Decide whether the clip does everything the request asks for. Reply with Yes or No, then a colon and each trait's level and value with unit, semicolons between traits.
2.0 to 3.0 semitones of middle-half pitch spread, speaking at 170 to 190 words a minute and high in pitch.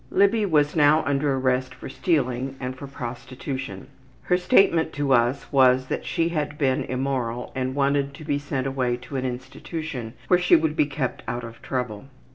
No: average, 2.7 semitones; average, 180 wpm; low, 135 Hz